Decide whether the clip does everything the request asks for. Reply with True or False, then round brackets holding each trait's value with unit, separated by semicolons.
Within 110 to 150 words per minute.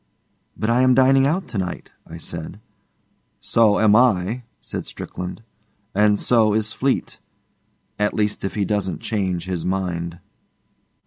True (140 wpm)